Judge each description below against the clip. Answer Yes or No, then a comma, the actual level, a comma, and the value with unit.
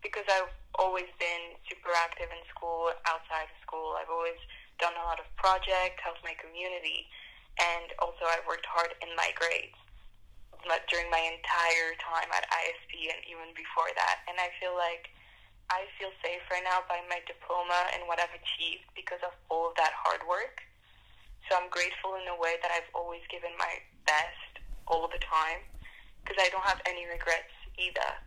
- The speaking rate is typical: Yes, average, 180 wpm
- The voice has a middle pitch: Yes, medium, 170 Hz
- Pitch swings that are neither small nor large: No, narrow, 1.4 semitones